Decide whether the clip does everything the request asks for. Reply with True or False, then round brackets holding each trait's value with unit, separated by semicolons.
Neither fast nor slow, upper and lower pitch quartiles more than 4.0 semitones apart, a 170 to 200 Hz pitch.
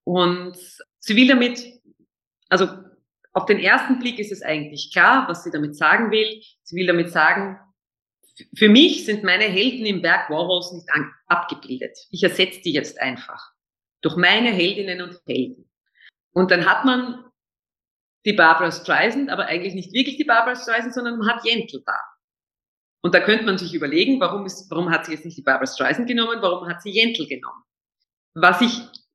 True (175 wpm; 5.2 semitones; 190 Hz)